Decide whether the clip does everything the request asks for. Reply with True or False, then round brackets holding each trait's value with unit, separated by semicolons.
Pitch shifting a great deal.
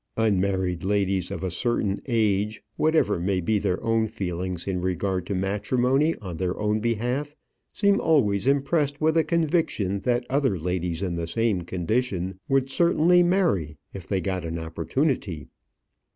True (6.6 semitones)